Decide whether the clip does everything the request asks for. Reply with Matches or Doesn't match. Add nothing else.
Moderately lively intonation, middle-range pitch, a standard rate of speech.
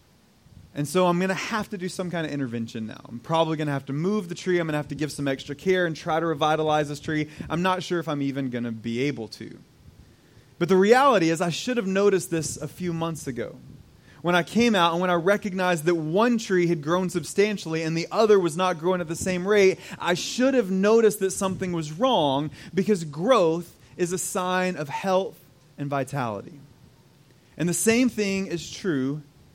Doesn't match